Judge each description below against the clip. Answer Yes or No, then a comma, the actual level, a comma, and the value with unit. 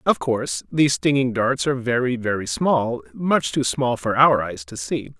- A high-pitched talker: No, low, 120 Hz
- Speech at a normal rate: Yes, average, 195 wpm